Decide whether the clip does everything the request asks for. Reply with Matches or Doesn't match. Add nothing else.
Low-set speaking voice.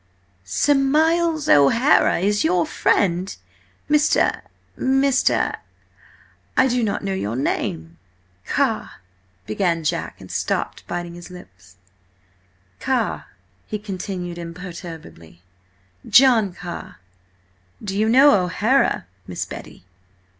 Doesn't match